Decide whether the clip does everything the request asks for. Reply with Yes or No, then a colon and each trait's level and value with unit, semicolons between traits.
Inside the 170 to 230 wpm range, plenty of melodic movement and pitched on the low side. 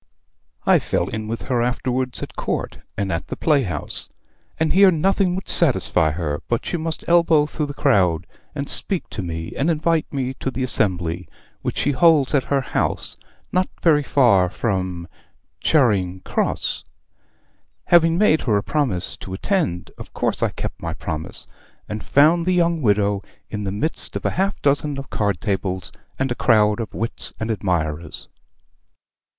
Yes: average, 175 wpm; wide, 8.4 semitones; low, 125 Hz